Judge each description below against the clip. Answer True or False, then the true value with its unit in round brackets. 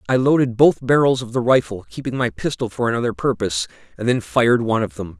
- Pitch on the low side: True (125 Hz)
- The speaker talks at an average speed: False (220 wpm)